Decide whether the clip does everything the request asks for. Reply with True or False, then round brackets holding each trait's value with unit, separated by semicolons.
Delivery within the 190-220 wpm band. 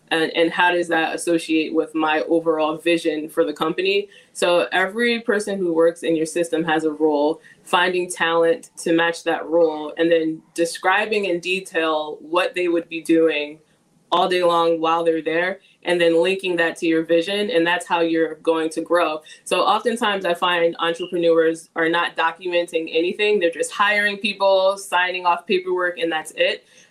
False (175 wpm)